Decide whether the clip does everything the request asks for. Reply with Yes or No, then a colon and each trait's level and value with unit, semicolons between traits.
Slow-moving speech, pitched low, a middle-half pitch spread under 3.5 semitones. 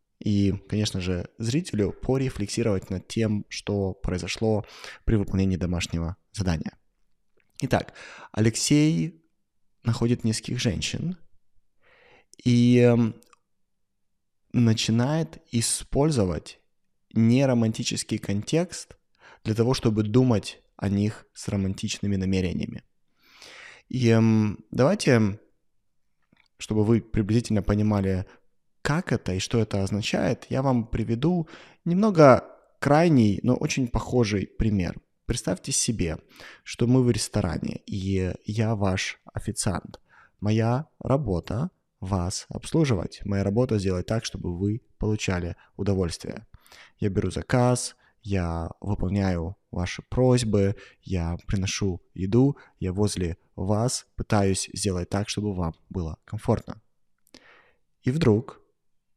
No: slow, 100 wpm; low, 105 Hz; average, 3.8 semitones